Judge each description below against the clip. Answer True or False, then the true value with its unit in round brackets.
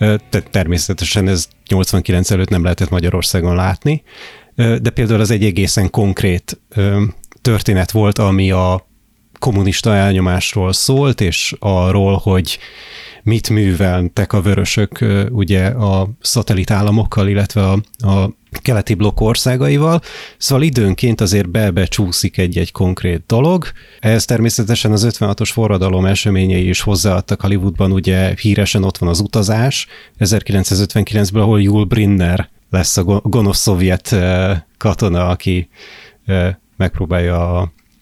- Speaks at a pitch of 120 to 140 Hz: False (100 Hz)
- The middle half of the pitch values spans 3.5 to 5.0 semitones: False (2.7 semitones)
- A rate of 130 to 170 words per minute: False (115 wpm)